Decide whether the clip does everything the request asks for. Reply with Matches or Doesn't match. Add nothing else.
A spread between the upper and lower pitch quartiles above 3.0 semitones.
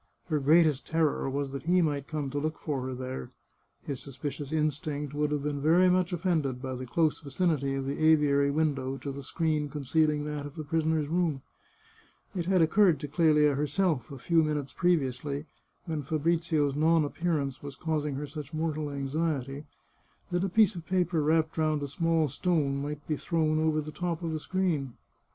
Doesn't match